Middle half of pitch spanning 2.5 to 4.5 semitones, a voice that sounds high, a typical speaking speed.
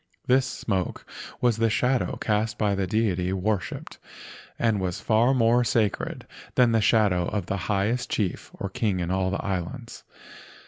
No: average, 3.3 semitones; low, 105 Hz; average, 155 wpm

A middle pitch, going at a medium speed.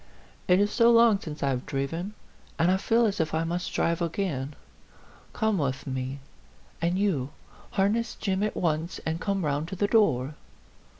Yes: medium, 175 Hz; average, 175 wpm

